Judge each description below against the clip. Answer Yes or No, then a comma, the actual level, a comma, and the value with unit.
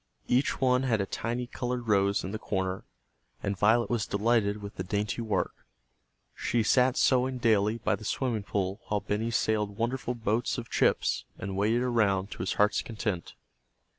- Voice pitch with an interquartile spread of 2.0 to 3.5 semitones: Yes, average, 3.1 semitones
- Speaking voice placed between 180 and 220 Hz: No, low, 110 Hz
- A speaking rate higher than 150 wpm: Yes, average, 170 wpm